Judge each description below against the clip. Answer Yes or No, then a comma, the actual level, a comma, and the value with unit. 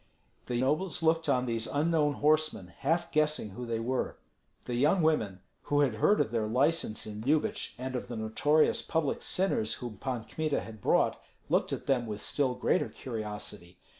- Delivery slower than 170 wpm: No, average, 175 wpm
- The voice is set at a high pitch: No, low, 130 Hz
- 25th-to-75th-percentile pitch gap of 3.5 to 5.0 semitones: No, wide, 5.6 semitones